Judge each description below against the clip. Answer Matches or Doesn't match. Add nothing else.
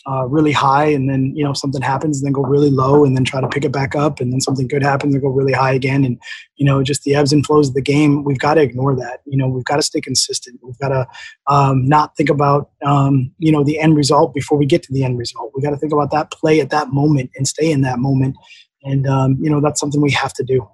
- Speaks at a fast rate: Matches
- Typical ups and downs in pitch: Doesn't match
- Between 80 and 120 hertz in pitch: Doesn't match